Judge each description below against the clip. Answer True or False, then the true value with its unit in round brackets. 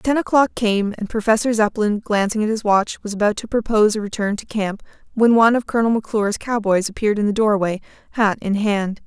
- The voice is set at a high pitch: True (215 Hz)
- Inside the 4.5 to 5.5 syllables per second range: False (6.1 syllables/s)